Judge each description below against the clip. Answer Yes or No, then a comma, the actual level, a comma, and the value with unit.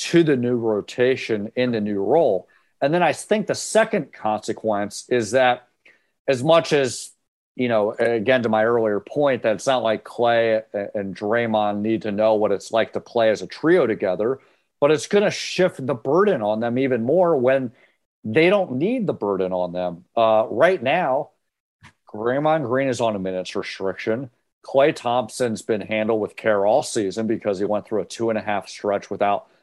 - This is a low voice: Yes, low, 115 Hz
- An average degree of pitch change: Yes, average, 3.7 semitones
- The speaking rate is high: No, average, 190 wpm